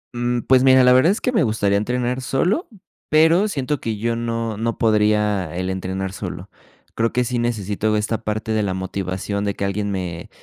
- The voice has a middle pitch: No, low, 110 Hz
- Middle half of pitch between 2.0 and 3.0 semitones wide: No, average, 3.8 semitones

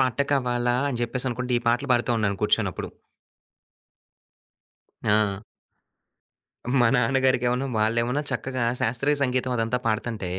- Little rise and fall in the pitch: Yes, narrow, 1.6 semitones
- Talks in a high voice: No, low, 125 Hz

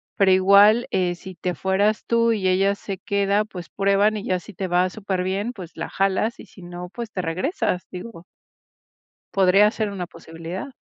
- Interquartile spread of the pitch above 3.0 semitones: No, narrow, 2.4 semitones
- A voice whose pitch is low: No, high, 195 Hz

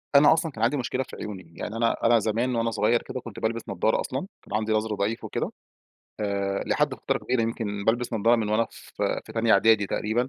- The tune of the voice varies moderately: No, narrow, 2.0 semitones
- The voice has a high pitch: No, low, 115 Hz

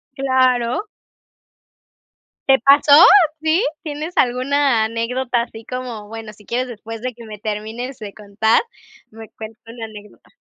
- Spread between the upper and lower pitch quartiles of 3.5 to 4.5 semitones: No, average, 2.9 semitones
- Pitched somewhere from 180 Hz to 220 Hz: No, high, 235 Hz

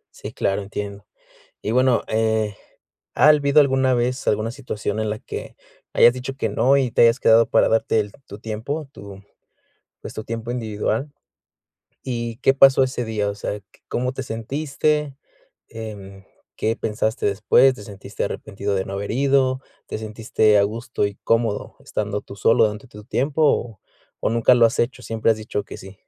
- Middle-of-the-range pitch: No, low, 115 Hz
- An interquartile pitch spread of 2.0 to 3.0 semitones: No, average, 3.6 semitones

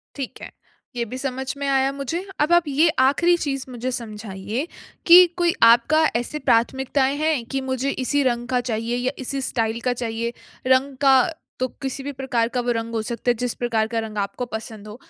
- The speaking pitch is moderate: No, very high, 255 Hz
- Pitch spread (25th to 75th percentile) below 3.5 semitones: Yes, average, 3.0 semitones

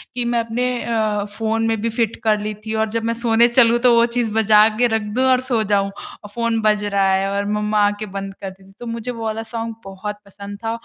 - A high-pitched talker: Yes, high, 220 Hz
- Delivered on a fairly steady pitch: Yes, narrow, 1.9 semitones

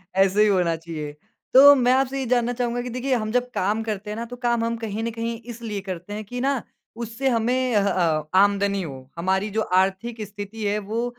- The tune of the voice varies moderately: Yes, average, 3.6 semitones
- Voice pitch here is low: No, high, 220 Hz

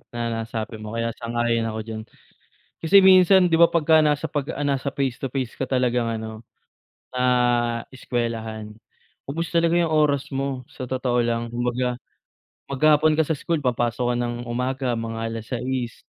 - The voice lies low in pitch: Yes, low, 125 Hz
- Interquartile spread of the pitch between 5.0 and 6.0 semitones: No, average, 3.5 semitones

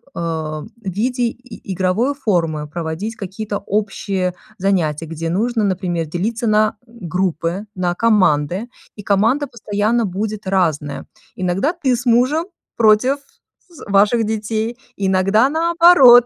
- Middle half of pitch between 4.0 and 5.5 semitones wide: Yes, average, 4.6 semitones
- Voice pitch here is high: Yes, high, 205 Hz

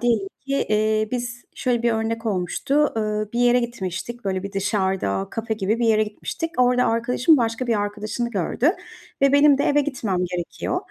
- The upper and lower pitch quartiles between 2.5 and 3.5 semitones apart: Yes, average, 3.0 semitones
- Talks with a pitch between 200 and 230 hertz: Yes, high, 225 Hz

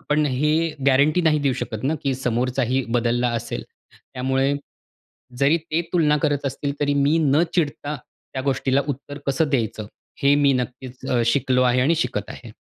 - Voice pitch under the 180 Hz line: Yes, medium, 140 Hz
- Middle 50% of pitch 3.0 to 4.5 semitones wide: No, narrow, 2.5 semitones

